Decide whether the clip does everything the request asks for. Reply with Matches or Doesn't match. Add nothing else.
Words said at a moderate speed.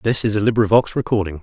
Doesn't match